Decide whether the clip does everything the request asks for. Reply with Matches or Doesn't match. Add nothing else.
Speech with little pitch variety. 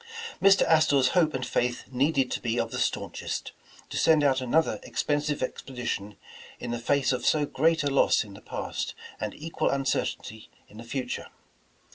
Doesn't match